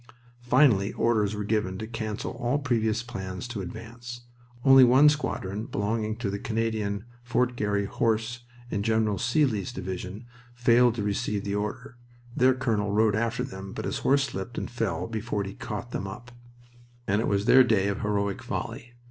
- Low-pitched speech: Yes, low, 110 Hz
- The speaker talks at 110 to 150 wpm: No, average, 170 wpm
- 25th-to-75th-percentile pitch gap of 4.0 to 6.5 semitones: No, average, 3.0 semitones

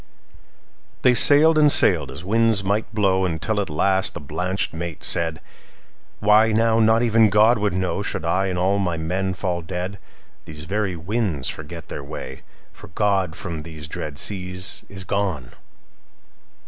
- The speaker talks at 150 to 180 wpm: No, average, 140 wpm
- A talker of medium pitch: No, very low, 95 Hz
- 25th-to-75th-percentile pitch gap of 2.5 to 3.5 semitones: No, average, 4.2 semitones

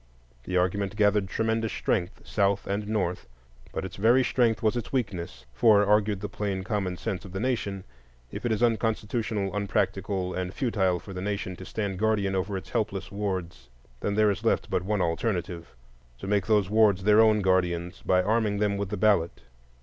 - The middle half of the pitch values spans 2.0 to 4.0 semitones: Yes, narrow, 2.6 semitones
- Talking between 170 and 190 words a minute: Yes, average, 180 wpm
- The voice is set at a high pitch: No, low, 100 Hz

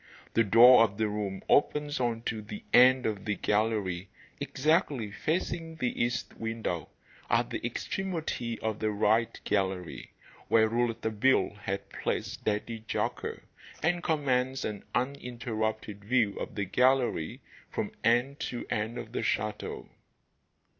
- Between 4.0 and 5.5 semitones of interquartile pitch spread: No, average, 3.3 semitones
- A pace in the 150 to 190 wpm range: No, slow, 135 wpm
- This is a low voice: Yes, low, 115 Hz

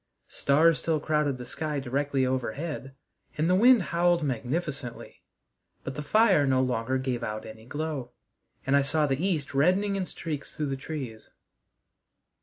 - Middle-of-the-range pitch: Yes, medium, 145 Hz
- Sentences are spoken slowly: No, average, 155 wpm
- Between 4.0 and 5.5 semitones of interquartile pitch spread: No, average, 3.6 semitones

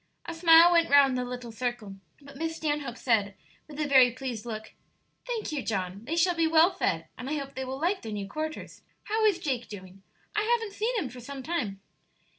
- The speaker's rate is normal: No, fast, 215 wpm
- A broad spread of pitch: Yes, wide, 5.7 semitones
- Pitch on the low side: No, very high, 275 Hz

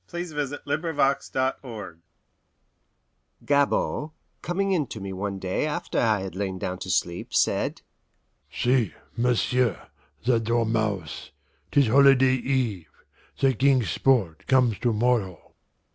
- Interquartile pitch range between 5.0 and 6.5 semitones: Yes, average, 5.3 semitones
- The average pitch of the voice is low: Yes, low, 120 Hz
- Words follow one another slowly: Yes, slow, 120 wpm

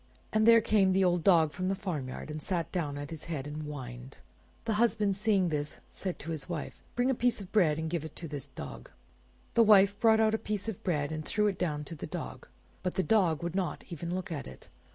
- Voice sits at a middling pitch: Yes, medium, 175 Hz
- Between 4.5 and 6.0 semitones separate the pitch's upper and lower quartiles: Yes, average, 5.3 semitones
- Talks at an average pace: No, fast, 240 wpm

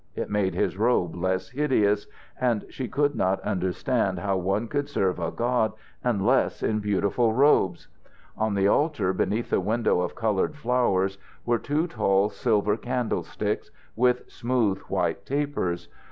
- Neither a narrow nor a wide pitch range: Yes, average, 4.6 semitones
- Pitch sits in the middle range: No, low, 110 Hz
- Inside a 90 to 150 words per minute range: Yes, average, 145 wpm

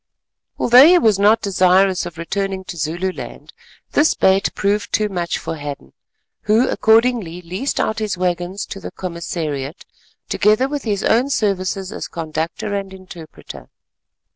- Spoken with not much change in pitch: No, average, 3.8 semitones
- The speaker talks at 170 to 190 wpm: No, average, 140 wpm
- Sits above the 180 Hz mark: Yes, high, 190 Hz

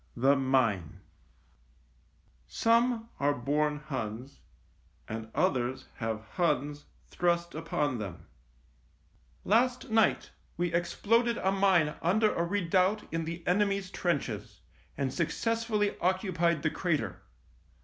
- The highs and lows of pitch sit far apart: Yes, wide, 6.6 semitones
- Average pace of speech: No, slow, 110 wpm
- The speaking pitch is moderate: Yes, medium, 170 Hz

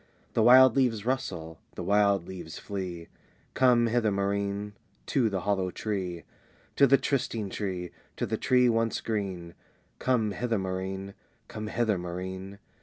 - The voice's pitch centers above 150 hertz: No, low, 100 Hz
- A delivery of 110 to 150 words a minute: Yes, average, 140 wpm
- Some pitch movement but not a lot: Yes, average, 3.8 semitones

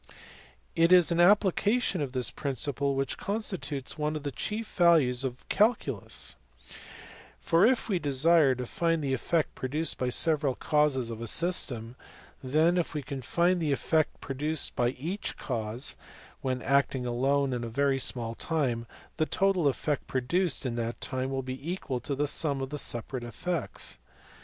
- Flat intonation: No, average, 4.5 semitones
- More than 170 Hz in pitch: No, medium, 140 Hz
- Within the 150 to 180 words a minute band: Yes, average, 170 wpm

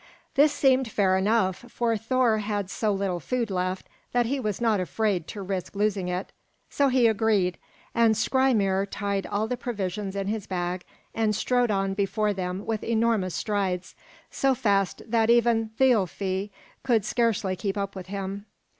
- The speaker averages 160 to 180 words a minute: Yes, average, 165 wpm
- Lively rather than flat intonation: No, average, 3.2 semitones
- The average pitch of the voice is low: No, high, 205 Hz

